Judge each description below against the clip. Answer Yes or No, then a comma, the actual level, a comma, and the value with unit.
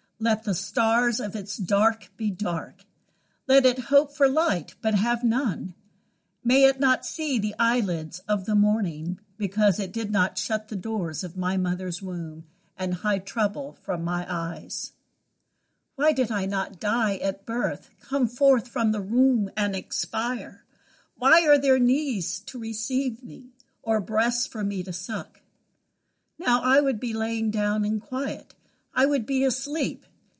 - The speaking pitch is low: No, high, 220 Hz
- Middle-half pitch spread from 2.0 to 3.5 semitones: No, average, 4.5 semitones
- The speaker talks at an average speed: Yes, average, 160 wpm